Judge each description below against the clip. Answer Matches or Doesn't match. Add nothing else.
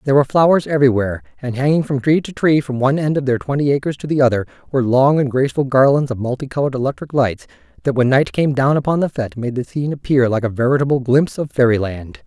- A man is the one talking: Matches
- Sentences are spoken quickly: Matches